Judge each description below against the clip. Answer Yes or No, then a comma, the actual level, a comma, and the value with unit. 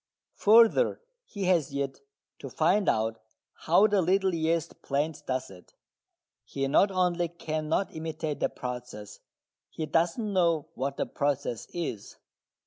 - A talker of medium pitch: Yes, medium, 160 Hz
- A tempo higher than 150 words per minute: No, slow, 135 wpm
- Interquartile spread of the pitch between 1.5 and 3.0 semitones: No, average, 4.9 semitones